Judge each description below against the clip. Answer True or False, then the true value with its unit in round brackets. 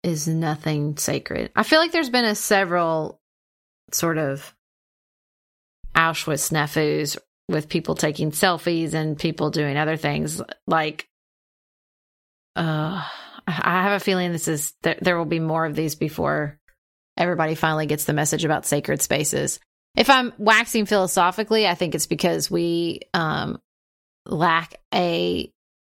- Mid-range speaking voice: True (160 Hz)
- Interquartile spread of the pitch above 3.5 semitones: False (2.9 semitones)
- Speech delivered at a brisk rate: False (135 wpm)